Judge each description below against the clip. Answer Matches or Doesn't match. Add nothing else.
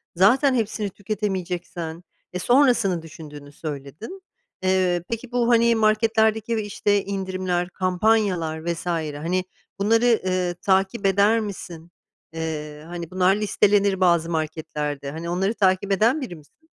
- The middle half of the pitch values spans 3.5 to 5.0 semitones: Matches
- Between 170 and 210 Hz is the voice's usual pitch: Matches